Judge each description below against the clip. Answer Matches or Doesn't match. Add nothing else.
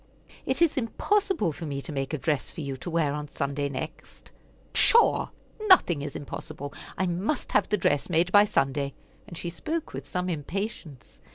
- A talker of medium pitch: Matches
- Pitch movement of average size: Doesn't match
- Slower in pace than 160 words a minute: Doesn't match